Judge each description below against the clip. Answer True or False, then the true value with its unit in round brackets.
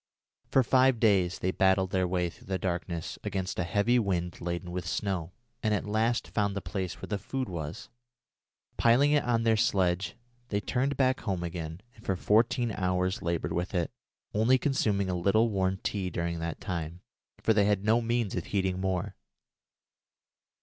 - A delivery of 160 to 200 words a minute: True (175 wpm)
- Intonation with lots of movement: False (3.9 semitones)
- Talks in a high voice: False (95 Hz)